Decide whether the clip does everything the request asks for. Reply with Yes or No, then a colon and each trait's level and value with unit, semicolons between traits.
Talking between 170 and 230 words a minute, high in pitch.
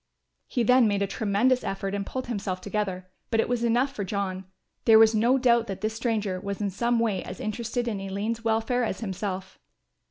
Yes: average, 200 wpm; high, 215 Hz